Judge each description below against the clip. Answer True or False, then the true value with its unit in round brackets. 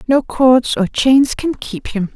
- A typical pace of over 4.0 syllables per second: False (3.6 syllables/s)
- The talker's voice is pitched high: True (250 Hz)